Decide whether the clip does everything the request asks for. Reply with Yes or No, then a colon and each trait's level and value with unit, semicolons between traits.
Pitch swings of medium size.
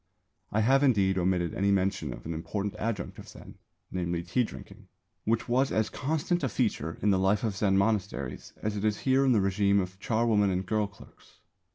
Yes: average, 3.0 semitones